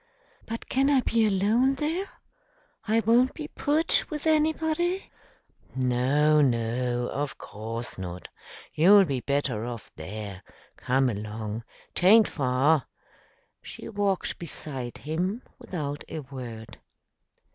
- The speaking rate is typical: No, slow, 115 wpm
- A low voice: No, medium, 150 Hz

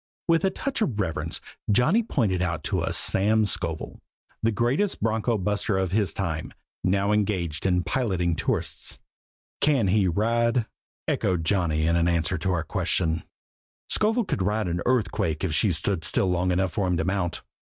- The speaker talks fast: No, average, 165 wpm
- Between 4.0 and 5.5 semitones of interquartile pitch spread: Yes, average, 4.3 semitones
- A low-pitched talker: Yes, very low, 95 Hz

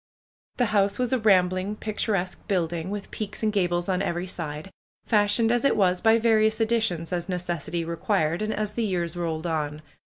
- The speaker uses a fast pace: No, average, 175 wpm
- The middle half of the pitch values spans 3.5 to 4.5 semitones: Yes, average, 3.8 semitones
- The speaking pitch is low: No, high, 190 Hz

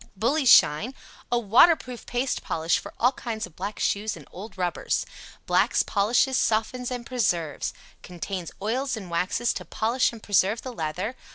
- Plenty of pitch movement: No, average, 5.0 semitones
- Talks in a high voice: Yes, high, 220 Hz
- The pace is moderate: Yes, average, 160 wpm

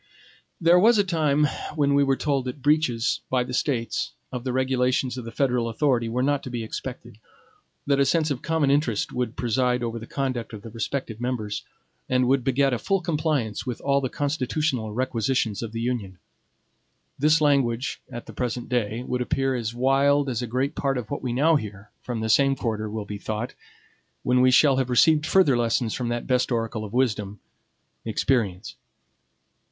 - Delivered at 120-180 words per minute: No, average, 190 wpm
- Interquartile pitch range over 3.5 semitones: No, average, 3.2 semitones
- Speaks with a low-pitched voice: Yes, low, 125 Hz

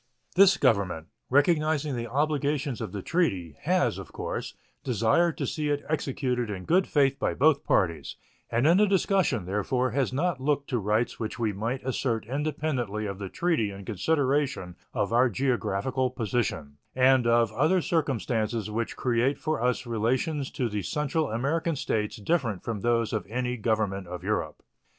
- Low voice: Yes, low, 125 Hz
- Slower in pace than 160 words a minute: No, average, 165 wpm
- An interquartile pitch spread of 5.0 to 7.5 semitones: Yes, average, 5.3 semitones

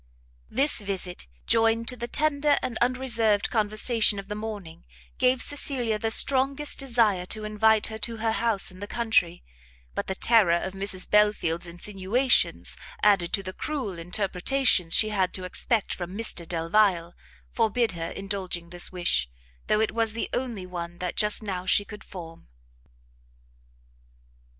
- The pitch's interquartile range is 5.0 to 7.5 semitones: No, average, 4.1 semitones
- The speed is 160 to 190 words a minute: No, average, 150 wpm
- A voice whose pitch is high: Yes, high, 210 Hz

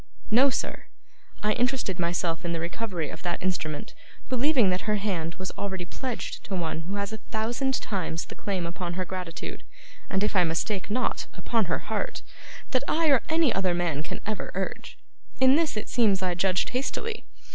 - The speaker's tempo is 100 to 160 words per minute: No, average, 185 wpm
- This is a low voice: No, high, 195 Hz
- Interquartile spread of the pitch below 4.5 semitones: No, average, 5.1 semitones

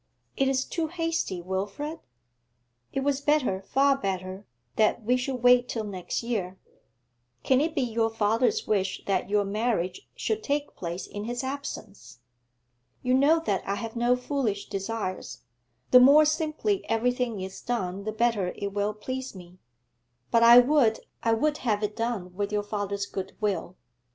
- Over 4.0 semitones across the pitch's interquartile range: Yes, average, 5.0 semitones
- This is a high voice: Yes, high, 230 Hz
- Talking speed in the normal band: Yes, average, 160 wpm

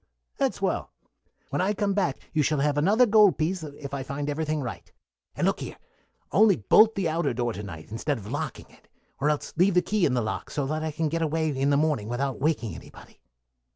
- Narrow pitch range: No, average, 3.9 semitones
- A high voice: No, medium, 150 Hz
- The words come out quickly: Yes, fast, 225 wpm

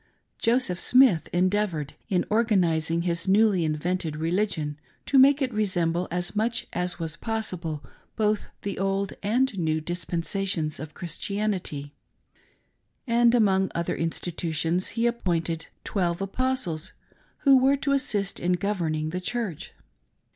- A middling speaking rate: No, slow, 125 wpm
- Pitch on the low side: No, medium, 185 Hz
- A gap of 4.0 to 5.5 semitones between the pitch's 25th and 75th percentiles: Yes, average, 4.5 semitones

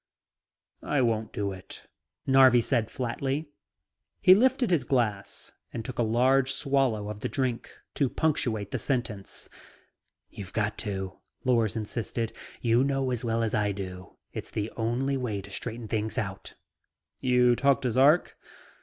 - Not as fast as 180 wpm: Yes, average, 150 wpm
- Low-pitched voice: Yes, low, 120 Hz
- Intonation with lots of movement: No, average, 3.9 semitones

